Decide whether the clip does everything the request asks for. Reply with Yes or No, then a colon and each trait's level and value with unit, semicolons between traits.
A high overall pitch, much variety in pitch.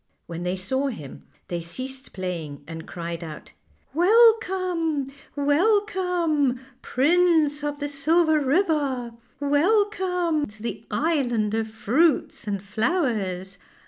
Yes: very high, 280 Hz; wide, 8.3 semitones